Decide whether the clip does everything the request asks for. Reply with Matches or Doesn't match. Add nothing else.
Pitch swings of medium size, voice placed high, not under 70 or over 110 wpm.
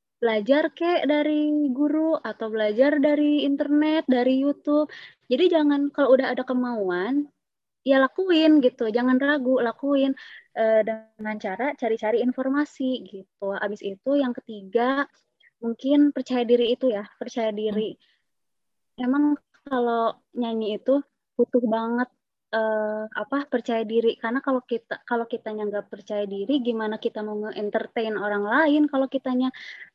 Doesn't match